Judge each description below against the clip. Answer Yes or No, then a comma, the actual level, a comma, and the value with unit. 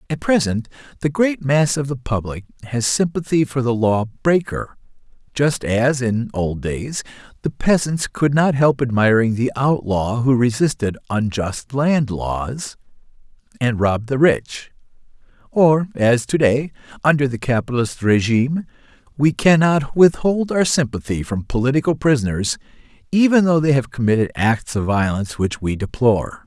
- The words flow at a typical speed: Yes, average, 145 wpm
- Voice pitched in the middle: No, low, 130 Hz